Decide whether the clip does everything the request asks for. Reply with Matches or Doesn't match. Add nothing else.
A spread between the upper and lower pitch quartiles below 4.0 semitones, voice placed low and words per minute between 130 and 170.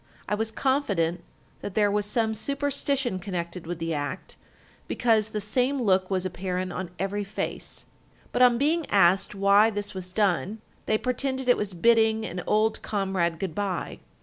Doesn't match